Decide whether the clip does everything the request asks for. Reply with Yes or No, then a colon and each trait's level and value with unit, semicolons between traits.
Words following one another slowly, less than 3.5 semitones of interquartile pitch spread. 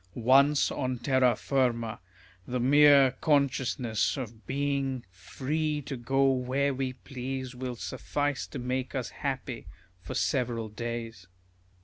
Yes: slow, 120 wpm; narrow, 2.4 semitones